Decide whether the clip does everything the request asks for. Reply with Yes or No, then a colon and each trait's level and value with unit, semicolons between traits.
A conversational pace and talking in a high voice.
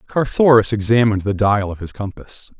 No: average, 160 wpm; low, 110 Hz